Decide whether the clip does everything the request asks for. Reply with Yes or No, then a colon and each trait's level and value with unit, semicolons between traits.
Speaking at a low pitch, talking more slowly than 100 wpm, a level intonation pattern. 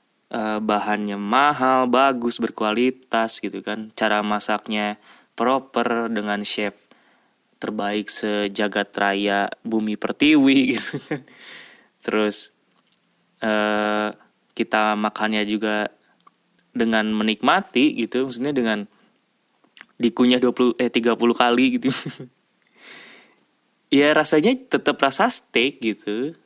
No: low, 110 Hz; average, 90 wpm; average, 3.4 semitones